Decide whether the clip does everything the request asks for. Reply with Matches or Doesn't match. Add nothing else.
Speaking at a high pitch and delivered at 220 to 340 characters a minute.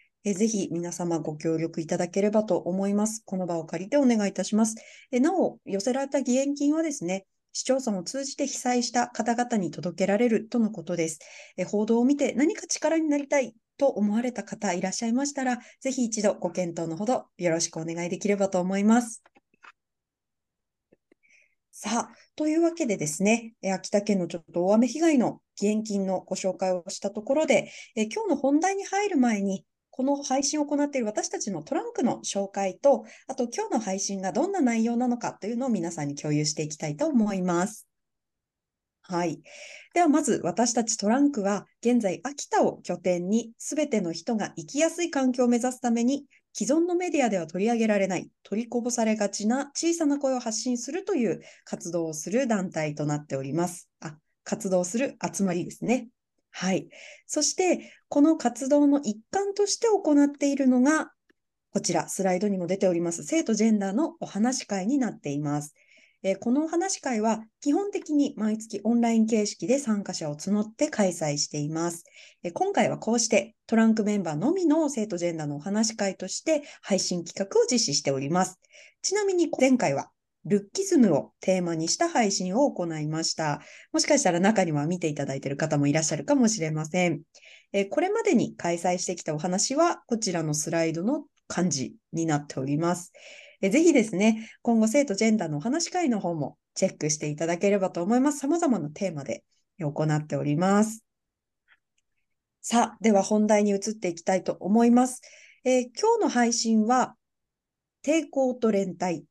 Doesn't match